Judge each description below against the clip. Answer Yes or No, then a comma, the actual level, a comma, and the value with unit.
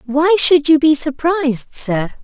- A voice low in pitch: No, very high, 295 Hz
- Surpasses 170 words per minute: No, average, 160 wpm